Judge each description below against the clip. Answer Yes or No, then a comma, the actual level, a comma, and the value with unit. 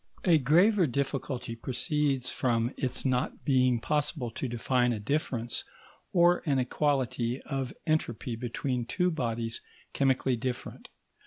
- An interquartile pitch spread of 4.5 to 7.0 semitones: No, average, 3.4 semitones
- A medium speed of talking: No, slow, 125 wpm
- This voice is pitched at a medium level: No, low, 130 Hz